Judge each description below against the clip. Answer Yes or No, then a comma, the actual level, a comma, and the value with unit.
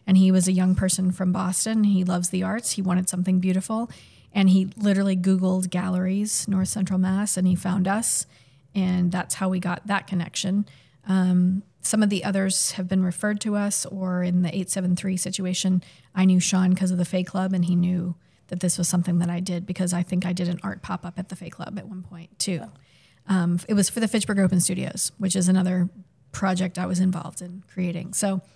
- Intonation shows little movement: Yes, narrow, 1.2 semitones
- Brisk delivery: Yes, fast, 220 wpm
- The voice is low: No, medium, 185 Hz